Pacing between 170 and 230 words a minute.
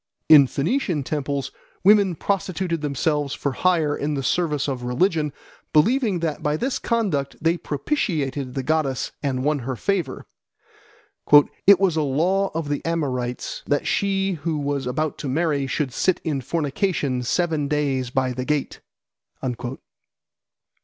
No: average, 140 wpm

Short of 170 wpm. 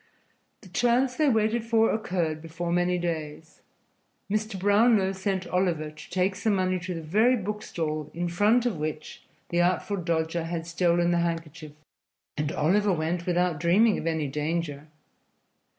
Yes: average, 155 wpm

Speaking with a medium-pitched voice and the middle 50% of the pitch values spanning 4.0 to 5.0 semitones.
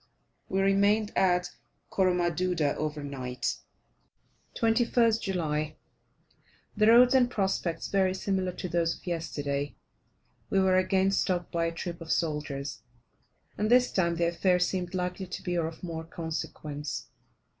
No: medium, 180 Hz; average, 3.0 semitones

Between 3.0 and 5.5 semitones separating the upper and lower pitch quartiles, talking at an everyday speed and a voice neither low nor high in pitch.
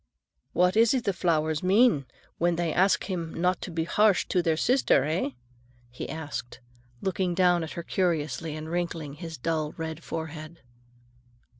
No: narrow, 2.6 semitones; average, 160 wpm; medium, 170 Hz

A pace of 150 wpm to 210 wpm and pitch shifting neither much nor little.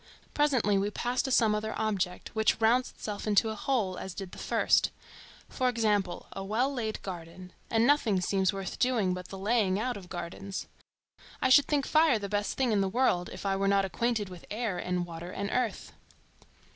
Yes: average, 195 wpm; average, 4.0 semitones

